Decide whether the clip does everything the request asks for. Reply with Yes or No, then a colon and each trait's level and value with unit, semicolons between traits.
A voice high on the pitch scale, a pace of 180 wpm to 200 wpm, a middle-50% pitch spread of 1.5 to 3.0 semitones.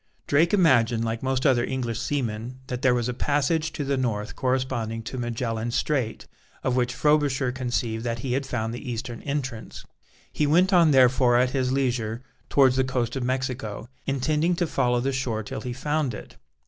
No: low, 130 Hz; average, 185 wpm; narrow, 2.5 semitones